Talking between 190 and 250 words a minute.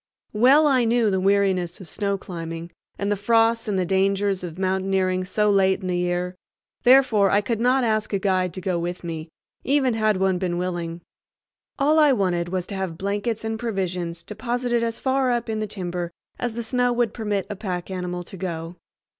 Yes: average, 195 wpm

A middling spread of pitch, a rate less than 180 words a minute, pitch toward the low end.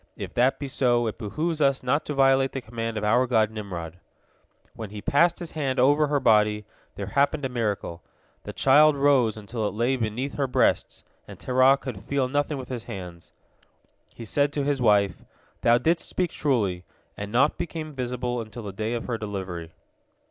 No: average, 4.6 semitones; average, 190 wpm; low, 125 Hz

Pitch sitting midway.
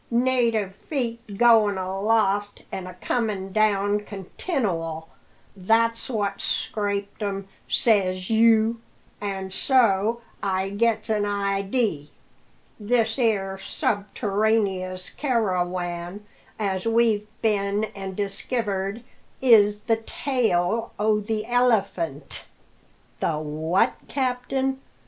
No: high, 205 Hz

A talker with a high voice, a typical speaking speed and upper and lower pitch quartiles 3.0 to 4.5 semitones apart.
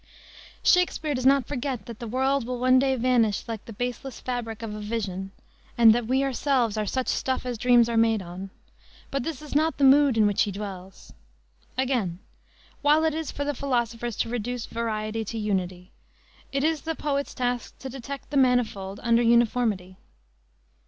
Yes: high, 240 Hz; average, 180 wpm; average, 3.8 semitones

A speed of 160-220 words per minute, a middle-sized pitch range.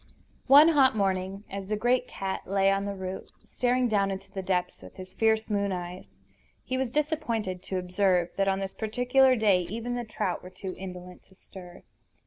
Yes: average, 190 wpm; average, 4.1 semitones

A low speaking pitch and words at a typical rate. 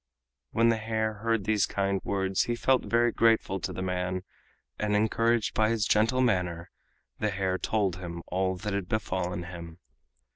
Yes: low, 100 Hz; average, 170 wpm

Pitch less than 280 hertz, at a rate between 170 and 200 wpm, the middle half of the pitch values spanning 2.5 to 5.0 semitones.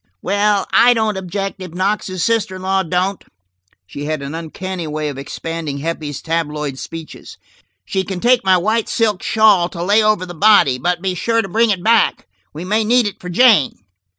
Yes: medium, 185 Hz; average, 190 wpm; average, 4.3 semitones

